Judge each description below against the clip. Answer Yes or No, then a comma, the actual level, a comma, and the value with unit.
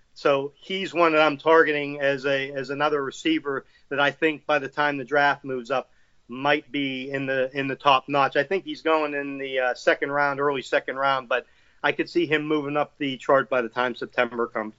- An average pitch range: No, narrow, 2.0 semitones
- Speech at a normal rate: No, fast, 225 wpm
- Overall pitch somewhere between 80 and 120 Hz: No, medium, 140 Hz